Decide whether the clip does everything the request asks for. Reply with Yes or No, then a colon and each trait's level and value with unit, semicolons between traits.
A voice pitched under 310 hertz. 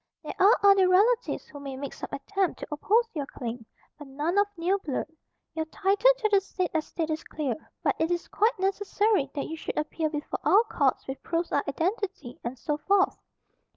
No: very high, 335 Hz